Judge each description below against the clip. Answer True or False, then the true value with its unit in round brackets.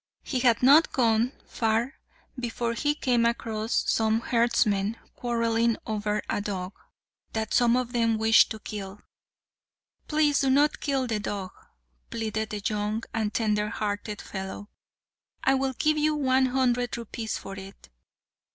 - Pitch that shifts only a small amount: False (3.0 semitones)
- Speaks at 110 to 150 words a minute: True (140 wpm)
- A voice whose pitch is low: False (230 Hz)